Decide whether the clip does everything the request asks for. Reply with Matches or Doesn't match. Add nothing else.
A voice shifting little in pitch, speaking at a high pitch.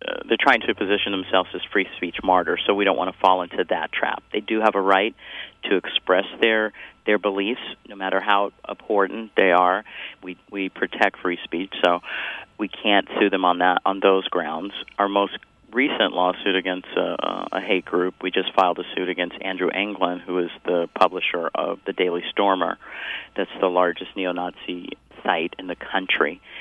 Doesn't match